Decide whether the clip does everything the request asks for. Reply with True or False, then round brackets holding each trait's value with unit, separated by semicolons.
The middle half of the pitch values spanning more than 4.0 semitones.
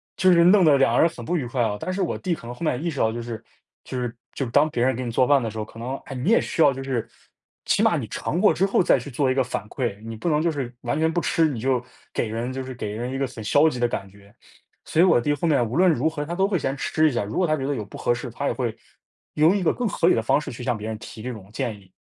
True (5.1 semitones)